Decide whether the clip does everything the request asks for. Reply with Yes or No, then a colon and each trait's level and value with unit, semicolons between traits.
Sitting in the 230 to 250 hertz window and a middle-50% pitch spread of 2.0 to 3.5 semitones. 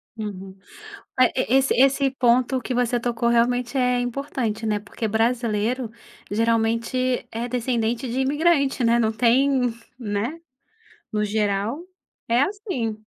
Yes: high, 240 Hz; narrow, 2.5 semitones